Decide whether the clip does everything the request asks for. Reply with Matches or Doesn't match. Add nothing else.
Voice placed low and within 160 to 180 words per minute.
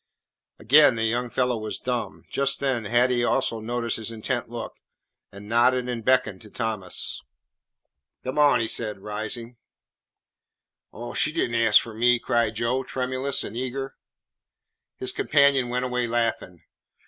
Doesn't match